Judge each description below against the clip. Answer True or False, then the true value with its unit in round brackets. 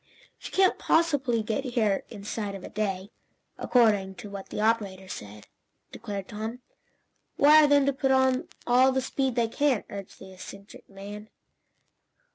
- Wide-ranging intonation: False (4.8 semitones)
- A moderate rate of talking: True (150 wpm)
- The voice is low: False (220 Hz)